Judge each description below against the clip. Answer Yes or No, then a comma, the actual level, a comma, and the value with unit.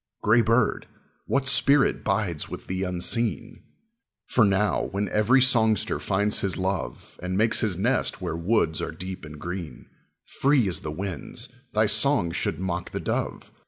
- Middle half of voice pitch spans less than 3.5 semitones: No, average, 4.2 semitones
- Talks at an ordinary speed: Yes, average, 160 wpm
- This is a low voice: Yes, low, 100 Hz